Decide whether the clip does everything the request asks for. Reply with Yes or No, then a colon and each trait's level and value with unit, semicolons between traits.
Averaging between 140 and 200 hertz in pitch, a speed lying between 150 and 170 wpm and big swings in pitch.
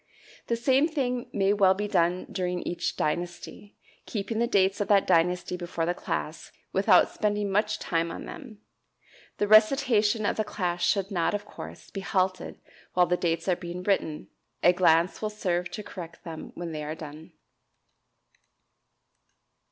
No: high, 190 Hz; average, 160 wpm; average, 3.3 semitones